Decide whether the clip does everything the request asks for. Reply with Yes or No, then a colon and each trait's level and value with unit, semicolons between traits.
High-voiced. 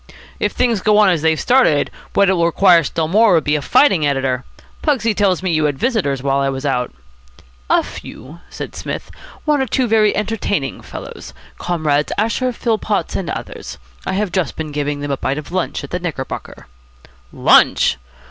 No: medium, 170 Hz